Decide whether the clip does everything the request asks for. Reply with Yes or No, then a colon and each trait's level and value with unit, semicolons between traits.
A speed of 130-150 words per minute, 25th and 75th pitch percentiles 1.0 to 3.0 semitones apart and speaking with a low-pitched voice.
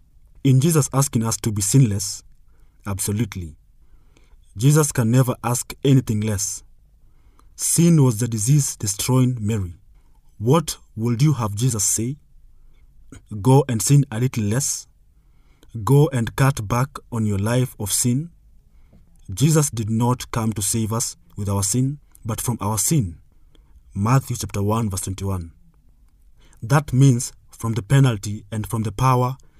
No: average, 140 wpm; average, 4.1 semitones; low, 115 Hz